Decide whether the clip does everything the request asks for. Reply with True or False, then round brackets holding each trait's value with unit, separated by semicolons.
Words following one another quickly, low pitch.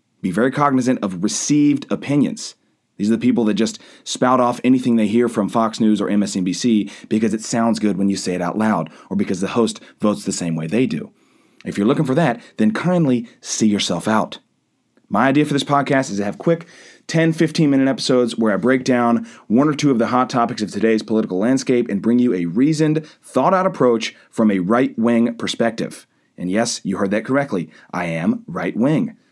True (210 wpm; 115 Hz)